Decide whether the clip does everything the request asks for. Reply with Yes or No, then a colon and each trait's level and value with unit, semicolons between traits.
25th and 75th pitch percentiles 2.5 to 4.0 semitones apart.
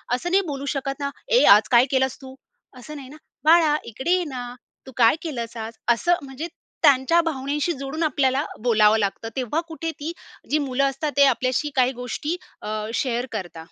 Yes: average, 3.6 semitones